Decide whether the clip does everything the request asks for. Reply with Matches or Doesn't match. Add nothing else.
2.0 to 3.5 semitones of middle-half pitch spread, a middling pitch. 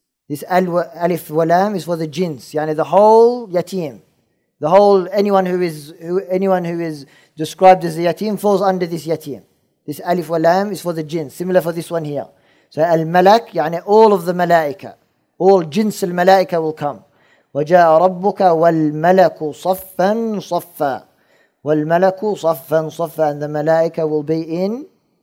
Matches